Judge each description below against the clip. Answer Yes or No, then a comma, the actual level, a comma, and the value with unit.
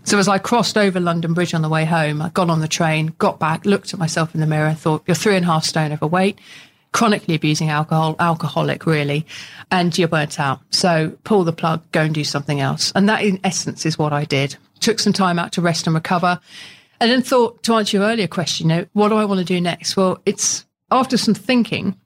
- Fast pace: Yes, fast, 240 wpm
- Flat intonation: No, average, 4.1 semitones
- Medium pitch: Yes, medium, 170 Hz